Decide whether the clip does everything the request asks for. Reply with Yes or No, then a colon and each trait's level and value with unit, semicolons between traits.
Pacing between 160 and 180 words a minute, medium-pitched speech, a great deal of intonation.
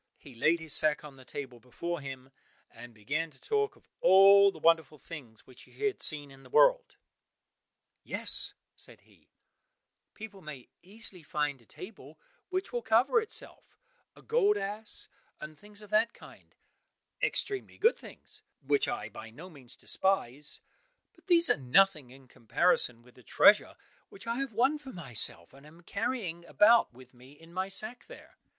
Yes: average, 165 wpm; medium, 170 Hz; wide, 8.8 semitones